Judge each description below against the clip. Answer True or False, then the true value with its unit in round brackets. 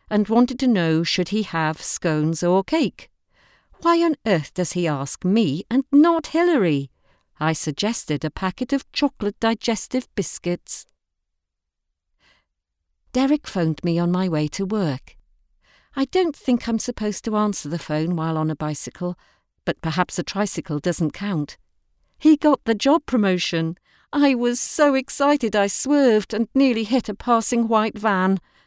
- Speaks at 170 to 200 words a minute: False (155 wpm)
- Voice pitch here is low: False (200 Hz)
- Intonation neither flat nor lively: False (7.3 semitones)